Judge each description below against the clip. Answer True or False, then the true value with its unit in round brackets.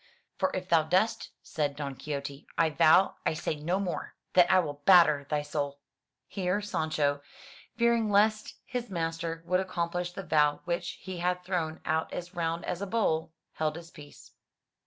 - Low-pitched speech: False (170 Hz)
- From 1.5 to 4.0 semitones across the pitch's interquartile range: True (3.2 semitones)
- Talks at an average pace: True (170 wpm)